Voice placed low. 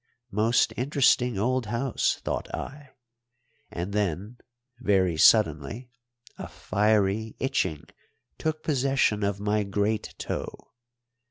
Yes: low, 110 Hz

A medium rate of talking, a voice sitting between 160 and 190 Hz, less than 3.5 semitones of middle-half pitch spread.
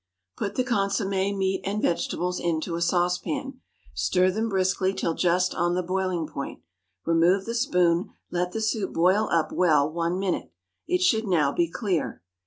Yes: average, 165 wpm; medium, 185 Hz; narrow, 2.6 semitones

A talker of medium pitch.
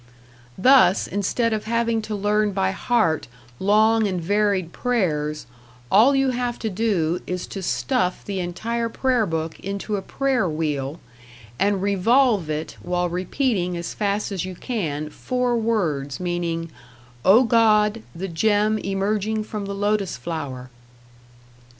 No: high, 200 Hz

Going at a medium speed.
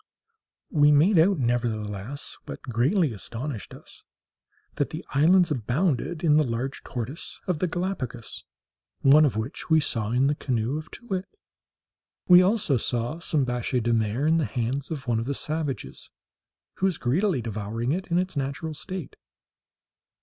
Yes: average, 160 wpm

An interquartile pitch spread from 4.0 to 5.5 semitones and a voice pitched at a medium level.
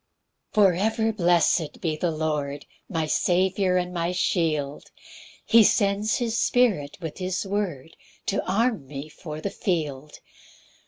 Yes: average, 4.5 semitones; medium, 180 Hz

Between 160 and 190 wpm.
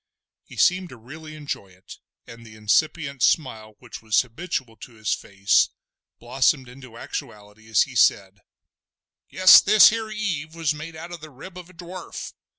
Yes: average, 165 wpm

